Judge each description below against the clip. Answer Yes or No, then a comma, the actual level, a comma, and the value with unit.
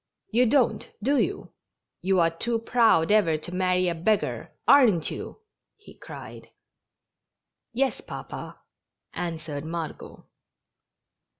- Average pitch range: No, wide, 6.2 semitones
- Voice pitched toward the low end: No, medium, 185 Hz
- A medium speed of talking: No, slow, 110 wpm